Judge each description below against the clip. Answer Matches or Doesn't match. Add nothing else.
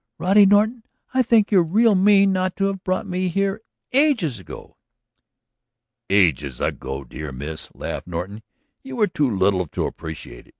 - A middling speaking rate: Matches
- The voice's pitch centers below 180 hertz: Doesn't match